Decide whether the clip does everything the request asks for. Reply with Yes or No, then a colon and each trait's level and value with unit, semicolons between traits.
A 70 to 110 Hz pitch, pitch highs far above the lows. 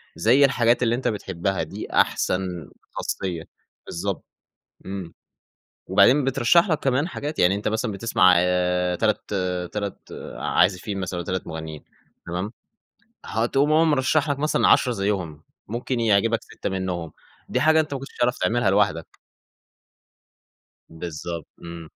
Yes: low, 100 Hz; wide, 5.9 semitones